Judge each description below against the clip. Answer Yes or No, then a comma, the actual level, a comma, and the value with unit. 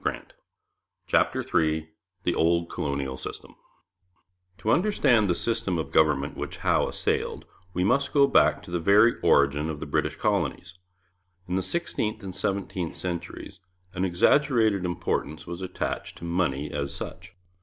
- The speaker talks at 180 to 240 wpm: No, average, 145 wpm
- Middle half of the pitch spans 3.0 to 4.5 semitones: No, average, 4.9 semitones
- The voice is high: No, very low, 90 Hz